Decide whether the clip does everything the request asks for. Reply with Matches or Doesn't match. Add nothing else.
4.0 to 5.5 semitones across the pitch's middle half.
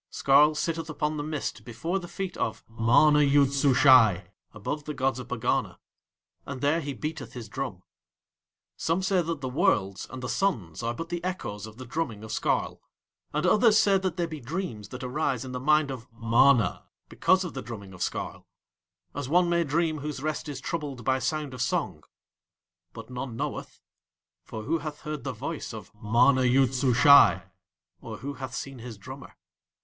Matches